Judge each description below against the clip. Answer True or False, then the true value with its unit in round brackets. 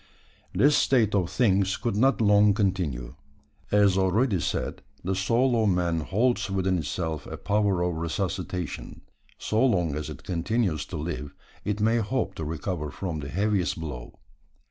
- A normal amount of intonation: True (4.2 semitones)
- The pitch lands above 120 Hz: False (95 Hz)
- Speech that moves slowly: False (155 wpm)